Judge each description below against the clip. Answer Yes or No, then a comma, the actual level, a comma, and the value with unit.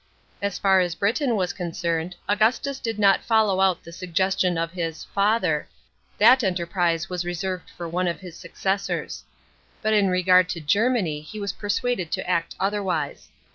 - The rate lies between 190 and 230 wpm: No, average, 170 wpm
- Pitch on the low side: No, medium, 185 Hz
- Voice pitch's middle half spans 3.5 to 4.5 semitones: No, average, 3.1 semitones